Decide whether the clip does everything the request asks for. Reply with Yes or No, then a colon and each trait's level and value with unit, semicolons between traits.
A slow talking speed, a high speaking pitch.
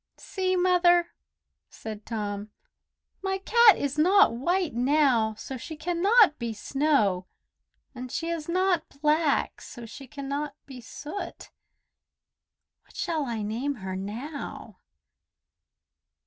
Yes: slow, 115 wpm; very high, 290 Hz